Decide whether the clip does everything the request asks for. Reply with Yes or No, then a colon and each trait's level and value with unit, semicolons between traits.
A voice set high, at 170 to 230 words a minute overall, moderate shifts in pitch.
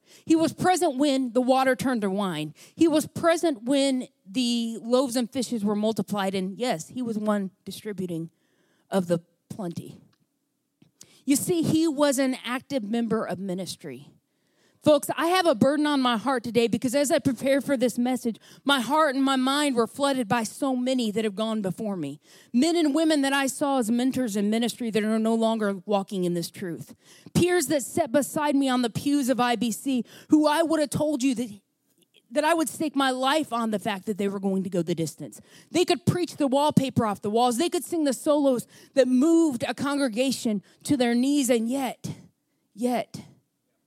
Yes: very high, 250 Hz; average, 195 wpm; average, 5.0 semitones